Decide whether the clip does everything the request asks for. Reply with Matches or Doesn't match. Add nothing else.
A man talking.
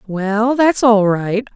Doesn't match